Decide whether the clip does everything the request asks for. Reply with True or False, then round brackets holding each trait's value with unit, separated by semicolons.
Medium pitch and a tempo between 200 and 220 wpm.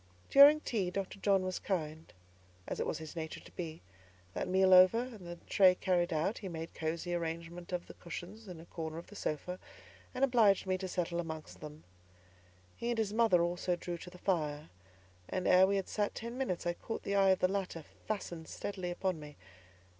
True (180 Hz; 205 wpm)